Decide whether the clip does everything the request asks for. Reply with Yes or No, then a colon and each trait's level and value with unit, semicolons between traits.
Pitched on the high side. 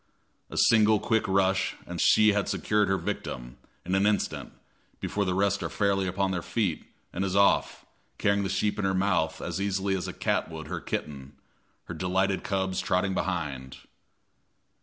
No: very low, 95 Hz